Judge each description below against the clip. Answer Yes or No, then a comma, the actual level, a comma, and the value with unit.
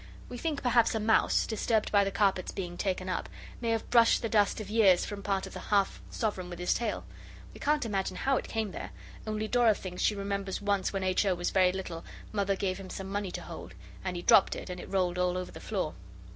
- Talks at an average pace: No, fast, 240 wpm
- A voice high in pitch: Yes, high, 200 Hz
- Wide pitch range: No, average, 2.9 semitones